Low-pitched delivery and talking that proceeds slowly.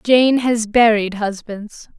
No: high, 220 Hz; slow, 120 wpm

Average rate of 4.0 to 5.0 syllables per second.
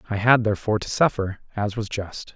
No: 5.9 syllables/s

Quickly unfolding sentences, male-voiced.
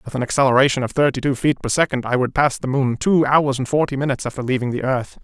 Yes: fast, 265 wpm; male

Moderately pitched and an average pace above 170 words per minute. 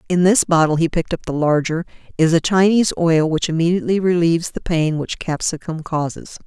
Yes: medium, 165 Hz; average, 185 wpm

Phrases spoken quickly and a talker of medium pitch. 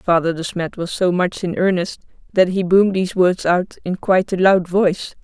Yes: fast, 220 wpm; medium, 180 Hz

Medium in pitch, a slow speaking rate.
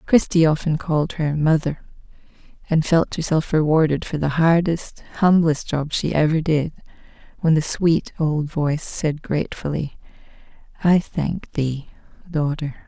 Yes: medium, 155 Hz; slow, 130 wpm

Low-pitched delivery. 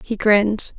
No: high, 210 Hz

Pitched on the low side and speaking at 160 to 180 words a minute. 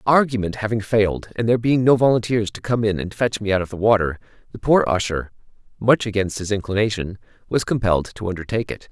No: low, 105 Hz; average, 200 wpm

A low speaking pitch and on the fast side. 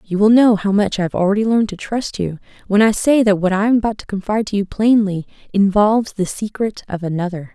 No: high, 205 Hz; fast, 240 wpm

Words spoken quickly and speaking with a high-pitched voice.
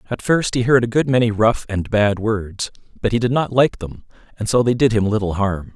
No: fast, 250 wpm; low, 110 Hz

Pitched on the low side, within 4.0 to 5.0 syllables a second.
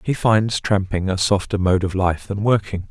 Yes: low, 100 Hz; 4.6 syllables/s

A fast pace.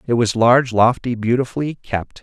No: average, 160 wpm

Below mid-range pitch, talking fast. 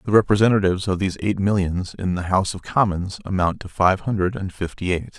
Yes: very low, 95 Hz; fast, 210 wpm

